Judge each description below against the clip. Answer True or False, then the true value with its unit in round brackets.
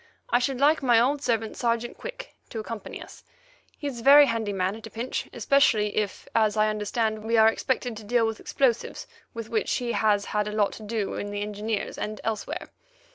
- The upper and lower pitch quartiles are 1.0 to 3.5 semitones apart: True (2.5 semitones)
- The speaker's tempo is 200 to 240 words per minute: True (205 wpm)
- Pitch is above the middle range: True (225 Hz)